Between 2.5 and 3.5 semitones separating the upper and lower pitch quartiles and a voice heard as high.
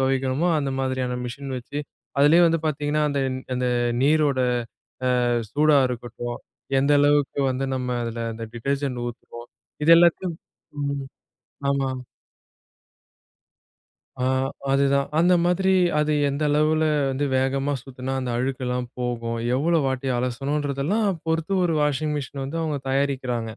No: average, 2.8 semitones; medium, 140 Hz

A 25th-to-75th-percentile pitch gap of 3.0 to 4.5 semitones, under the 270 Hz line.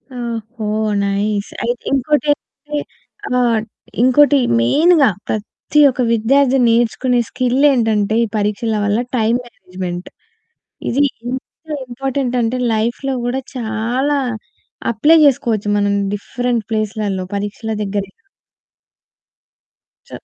Yes: average, 3.8 semitones; high, 235 Hz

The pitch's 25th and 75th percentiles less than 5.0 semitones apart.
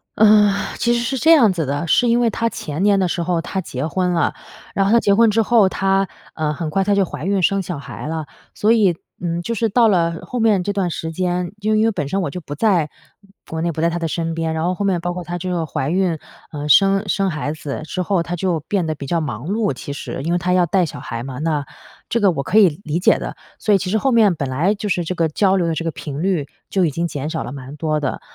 Yes: average, 3.9 semitones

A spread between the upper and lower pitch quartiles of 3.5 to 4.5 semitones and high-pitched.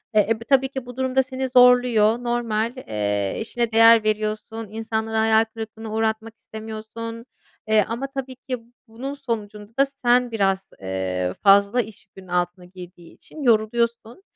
No: narrow, 2.5 semitones; high, 225 Hz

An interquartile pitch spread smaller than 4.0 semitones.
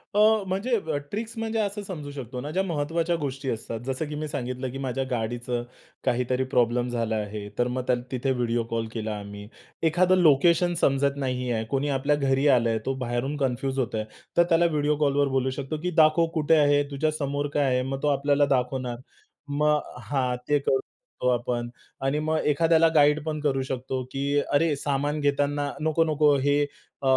Yes: average, 3.1 semitones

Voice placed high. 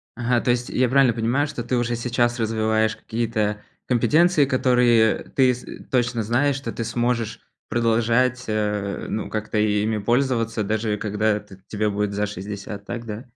No: low, 115 Hz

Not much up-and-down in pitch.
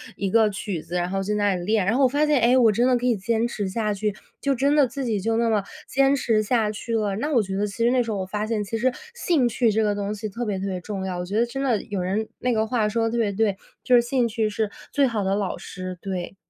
No: average, 3.2 semitones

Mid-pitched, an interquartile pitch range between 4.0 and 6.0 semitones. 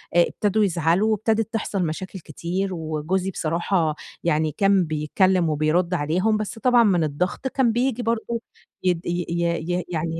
Yes: medium, 180 Hz; average, 4.5 semitones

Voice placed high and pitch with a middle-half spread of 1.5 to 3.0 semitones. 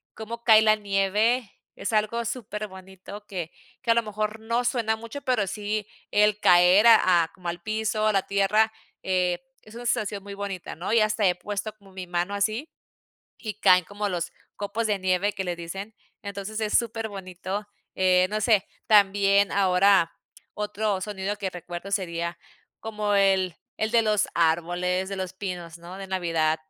Yes: high, 200 Hz; average, 2.7 semitones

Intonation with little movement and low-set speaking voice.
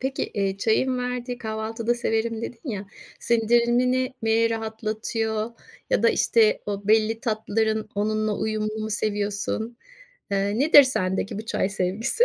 No: narrow, 1.8 semitones; high, 220 Hz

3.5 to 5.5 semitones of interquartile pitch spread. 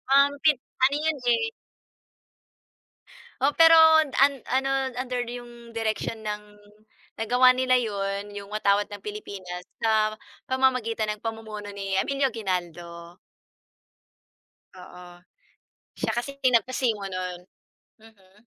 Yes: average, 4.2 semitones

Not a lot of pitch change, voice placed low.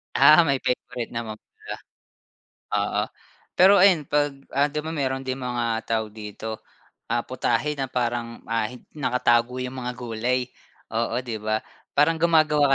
No: average, 3.8 semitones; low, 125 Hz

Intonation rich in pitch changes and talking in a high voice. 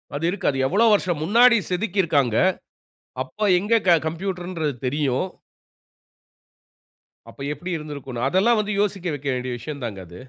No: wide, 6.3 semitones; medium, 165 Hz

